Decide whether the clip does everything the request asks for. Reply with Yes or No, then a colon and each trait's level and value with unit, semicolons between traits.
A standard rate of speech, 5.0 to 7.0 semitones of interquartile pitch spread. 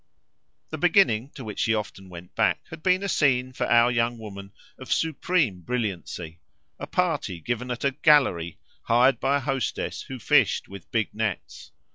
Yes: average, 170 wpm; wide, 5.6 semitones